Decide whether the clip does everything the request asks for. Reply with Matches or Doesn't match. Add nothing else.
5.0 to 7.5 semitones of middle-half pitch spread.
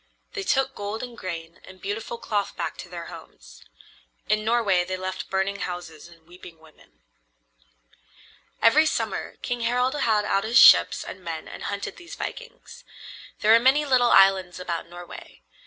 Matches